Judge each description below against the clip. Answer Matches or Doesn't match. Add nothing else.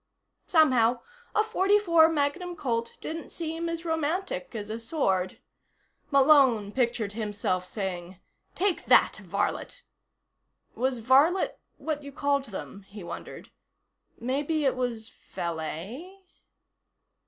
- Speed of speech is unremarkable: Doesn't match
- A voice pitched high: Matches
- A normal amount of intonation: Doesn't match